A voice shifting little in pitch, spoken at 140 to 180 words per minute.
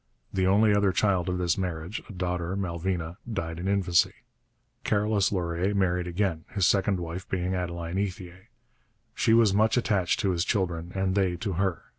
Yes: narrow, 2.3 semitones; average, 170 wpm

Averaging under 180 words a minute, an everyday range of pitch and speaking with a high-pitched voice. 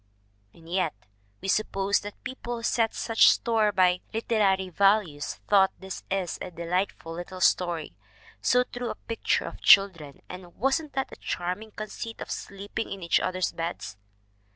Yes: average, 155 wpm; average, 3.7 semitones; high, 195 Hz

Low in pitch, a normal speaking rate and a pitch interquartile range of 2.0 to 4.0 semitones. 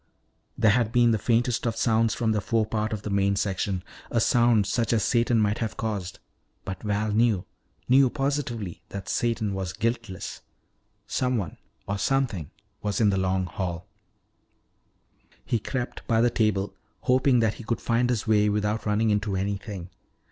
Yes: low, 110 Hz; average, 160 wpm; average, 2.8 semitones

